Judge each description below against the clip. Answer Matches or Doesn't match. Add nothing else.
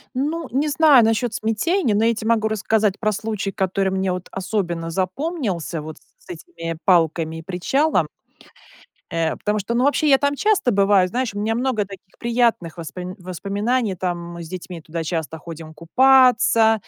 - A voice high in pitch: Matches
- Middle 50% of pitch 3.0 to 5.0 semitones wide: Doesn't match